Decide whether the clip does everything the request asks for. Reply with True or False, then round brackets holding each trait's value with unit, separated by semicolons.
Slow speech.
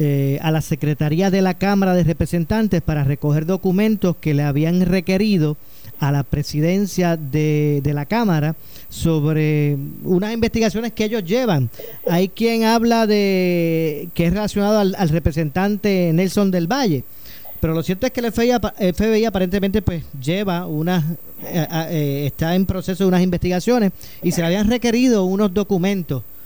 False (160 wpm)